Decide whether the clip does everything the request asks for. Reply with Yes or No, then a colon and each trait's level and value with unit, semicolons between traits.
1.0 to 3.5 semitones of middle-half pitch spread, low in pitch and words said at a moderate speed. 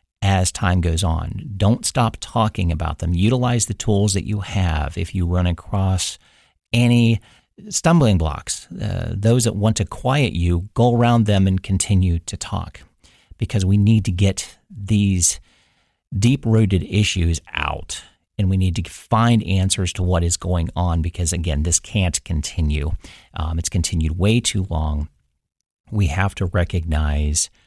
No: average, 4.0 semitones; very low, 95 Hz; average, 155 wpm